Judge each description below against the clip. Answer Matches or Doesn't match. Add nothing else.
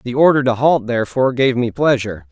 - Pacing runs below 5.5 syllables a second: Doesn't match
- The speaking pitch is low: Matches